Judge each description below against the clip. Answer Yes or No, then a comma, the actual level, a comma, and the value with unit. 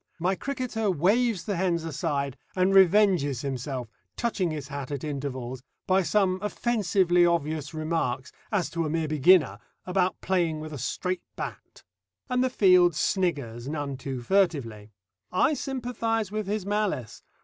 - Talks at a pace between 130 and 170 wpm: Yes, average, 145 wpm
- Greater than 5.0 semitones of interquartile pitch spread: Yes, wide, 5.6 semitones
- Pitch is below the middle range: No, medium, 170 Hz